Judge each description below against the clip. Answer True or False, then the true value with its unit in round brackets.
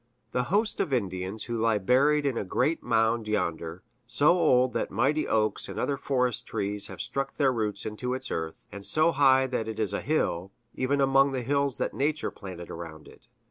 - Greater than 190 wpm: True (200 wpm)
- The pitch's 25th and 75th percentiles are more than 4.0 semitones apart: True (5.1 semitones)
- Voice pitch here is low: True (125 Hz)